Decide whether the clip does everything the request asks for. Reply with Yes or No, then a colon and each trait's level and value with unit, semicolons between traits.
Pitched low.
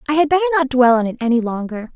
No: very high, 265 Hz